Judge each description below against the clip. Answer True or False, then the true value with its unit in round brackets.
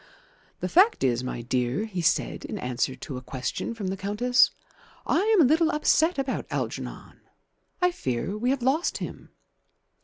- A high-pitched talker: True (220 Hz)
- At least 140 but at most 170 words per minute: True (165 wpm)